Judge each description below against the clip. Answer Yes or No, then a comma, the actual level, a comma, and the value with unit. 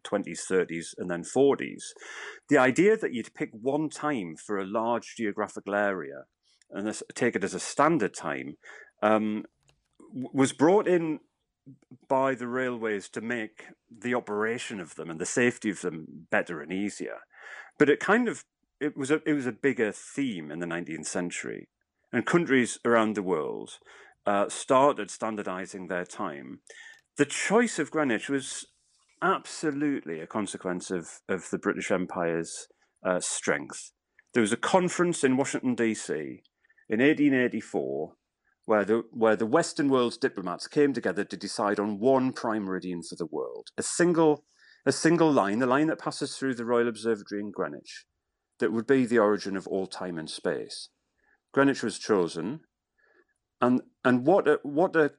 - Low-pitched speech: Yes, low, 125 Hz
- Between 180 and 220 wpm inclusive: No, average, 160 wpm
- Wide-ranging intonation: Yes, wide, 6.3 semitones